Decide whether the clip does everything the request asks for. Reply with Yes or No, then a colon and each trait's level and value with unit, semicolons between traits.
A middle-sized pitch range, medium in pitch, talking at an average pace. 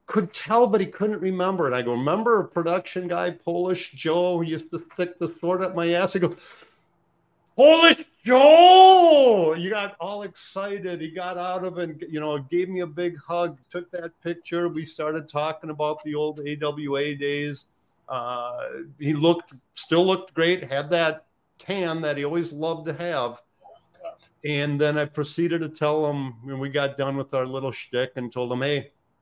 Yes: average, 3.5 semitones; medium, 170 Hz; average, 185 wpm